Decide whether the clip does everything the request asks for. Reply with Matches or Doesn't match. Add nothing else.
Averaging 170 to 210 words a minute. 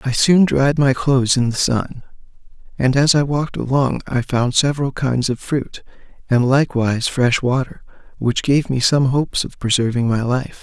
Matches